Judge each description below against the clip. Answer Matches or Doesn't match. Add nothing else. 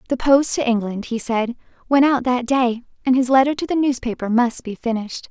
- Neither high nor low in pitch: Doesn't match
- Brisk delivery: Matches